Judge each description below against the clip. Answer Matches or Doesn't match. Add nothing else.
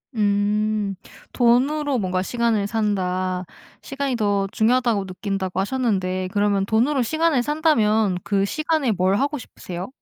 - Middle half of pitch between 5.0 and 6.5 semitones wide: Doesn't match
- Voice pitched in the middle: Doesn't match